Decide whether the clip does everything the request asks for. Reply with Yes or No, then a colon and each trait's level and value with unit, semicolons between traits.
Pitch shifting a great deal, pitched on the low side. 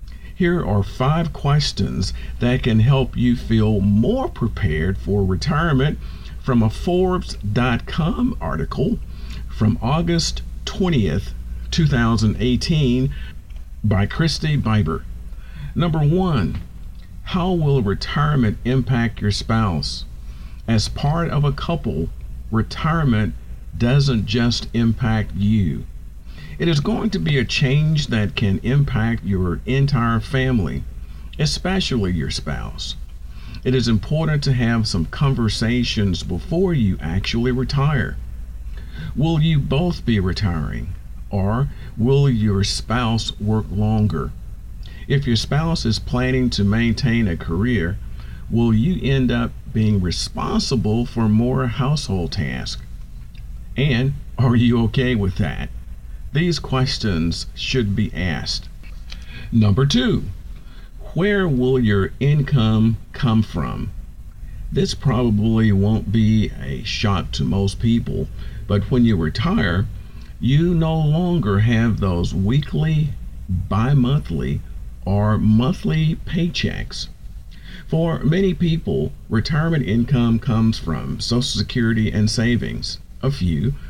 Yes: wide, 6.0 semitones; low, 115 Hz